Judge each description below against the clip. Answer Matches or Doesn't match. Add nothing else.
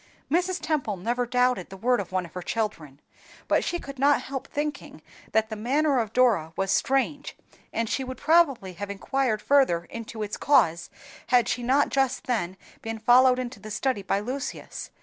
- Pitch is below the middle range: Doesn't match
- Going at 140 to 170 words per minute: Doesn't match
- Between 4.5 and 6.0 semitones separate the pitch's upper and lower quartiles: Matches